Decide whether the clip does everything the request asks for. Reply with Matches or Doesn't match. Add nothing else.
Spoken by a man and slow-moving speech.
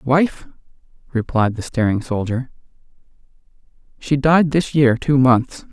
Matches